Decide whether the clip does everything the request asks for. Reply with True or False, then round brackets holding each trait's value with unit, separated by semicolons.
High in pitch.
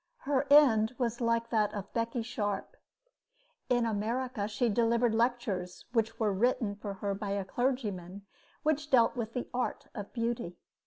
True (230 Hz)